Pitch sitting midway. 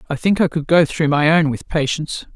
Yes: medium, 155 Hz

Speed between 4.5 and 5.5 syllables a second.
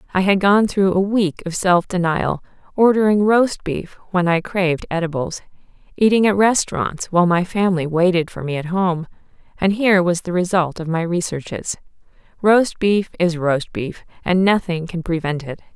Yes: 5.0 syllables/s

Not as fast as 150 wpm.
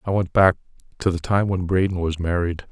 No: average, 200 wpm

